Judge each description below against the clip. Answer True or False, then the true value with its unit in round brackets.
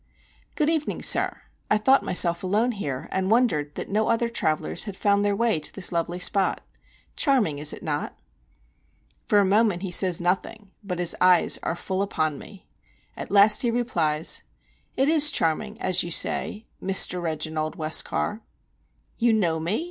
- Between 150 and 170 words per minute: True (165 wpm)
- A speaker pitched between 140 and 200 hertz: True (190 Hz)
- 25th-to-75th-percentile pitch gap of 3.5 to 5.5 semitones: True (4.6 semitones)